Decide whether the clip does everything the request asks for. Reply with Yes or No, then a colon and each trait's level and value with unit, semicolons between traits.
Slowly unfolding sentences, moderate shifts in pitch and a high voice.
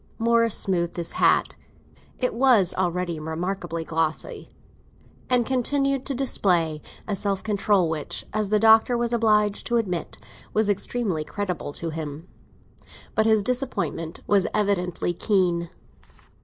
Yes: slow, 120 wpm; average, 5.0 semitones; high, 200 Hz